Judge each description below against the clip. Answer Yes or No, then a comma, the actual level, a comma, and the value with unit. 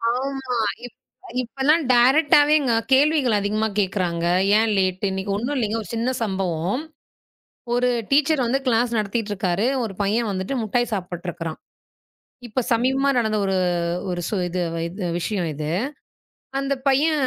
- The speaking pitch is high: Yes, high, 225 Hz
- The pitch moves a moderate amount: No, wide, 5.7 semitones